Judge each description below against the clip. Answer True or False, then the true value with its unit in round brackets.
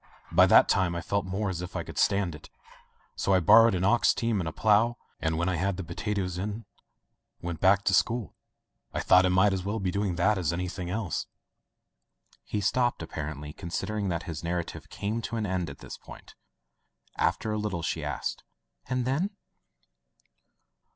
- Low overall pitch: True (95 Hz)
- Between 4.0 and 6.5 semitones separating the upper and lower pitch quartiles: False (3.4 semitones)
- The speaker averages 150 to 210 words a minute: True (190 wpm)